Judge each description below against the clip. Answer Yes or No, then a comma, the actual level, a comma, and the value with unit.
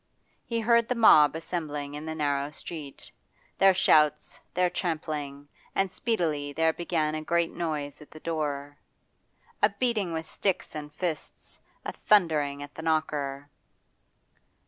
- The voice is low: No, medium, 155 Hz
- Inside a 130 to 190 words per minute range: Yes, average, 140 wpm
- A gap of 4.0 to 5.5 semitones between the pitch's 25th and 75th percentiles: No, average, 3.1 semitones